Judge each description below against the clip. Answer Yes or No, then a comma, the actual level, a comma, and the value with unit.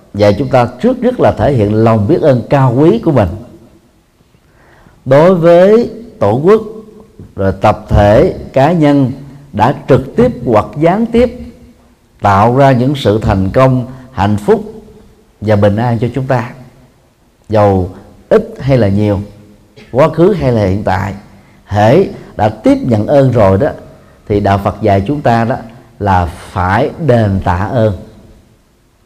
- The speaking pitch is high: No, low, 120 Hz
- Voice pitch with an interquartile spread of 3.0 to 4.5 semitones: No, wide, 5.4 semitones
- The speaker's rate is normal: No, slow, 155 wpm